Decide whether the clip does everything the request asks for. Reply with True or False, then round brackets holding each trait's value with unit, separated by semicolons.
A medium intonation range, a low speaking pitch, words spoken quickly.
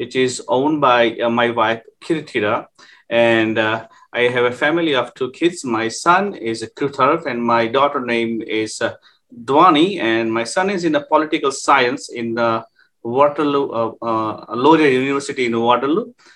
False (3.8 semitones; 120 Hz; 165 wpm)